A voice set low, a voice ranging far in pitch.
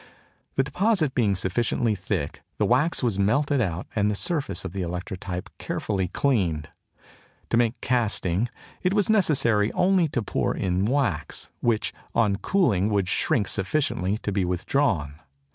Yes: low, 105 Hz; wide, 6.6 semitones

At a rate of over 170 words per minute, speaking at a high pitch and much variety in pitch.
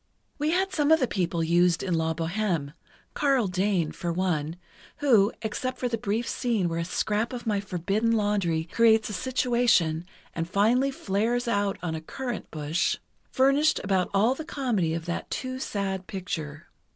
No: average, 165 wpm; high, 200 Hz; wide, 6.2 semitones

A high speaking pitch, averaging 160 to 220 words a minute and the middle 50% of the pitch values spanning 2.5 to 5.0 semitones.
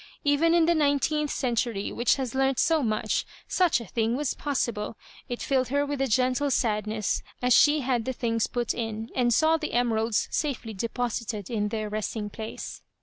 Yes: high, 245 Hz; average, 185 wpm; average, 4.2 semitones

